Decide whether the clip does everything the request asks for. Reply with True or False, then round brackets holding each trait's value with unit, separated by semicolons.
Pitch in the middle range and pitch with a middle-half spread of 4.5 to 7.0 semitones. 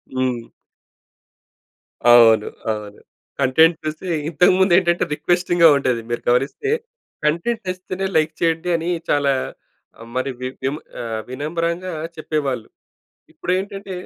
True (160 Hz; 5.5 semitones)